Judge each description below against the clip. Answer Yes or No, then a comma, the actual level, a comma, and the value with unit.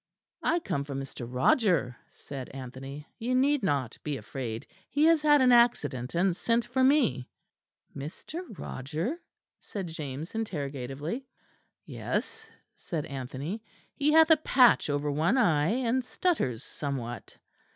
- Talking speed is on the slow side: Yes, slow, 130 wpm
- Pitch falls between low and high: Yes, medium, 160 Hz